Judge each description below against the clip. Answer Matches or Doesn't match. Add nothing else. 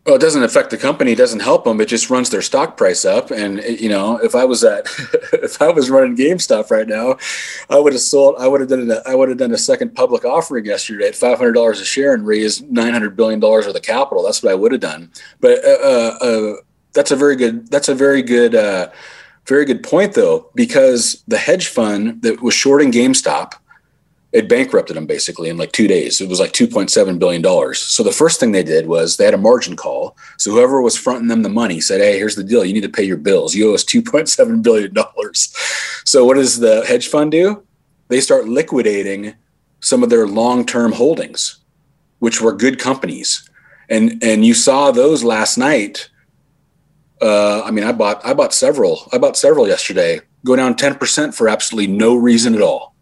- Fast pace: Matches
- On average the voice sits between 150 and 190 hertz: Matches